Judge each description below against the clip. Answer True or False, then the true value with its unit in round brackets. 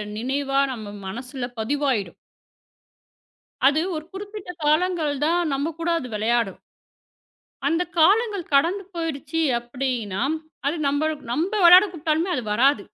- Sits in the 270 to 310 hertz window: True (290 Hz)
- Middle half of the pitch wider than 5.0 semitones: True (5.4 semitones)